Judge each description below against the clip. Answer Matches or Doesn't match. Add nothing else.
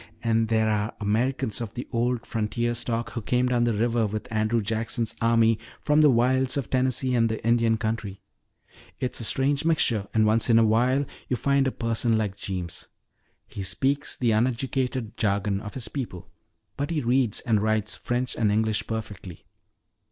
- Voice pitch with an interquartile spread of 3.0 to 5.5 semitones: Doesn't match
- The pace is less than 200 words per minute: Matches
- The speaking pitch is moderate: Doesn't match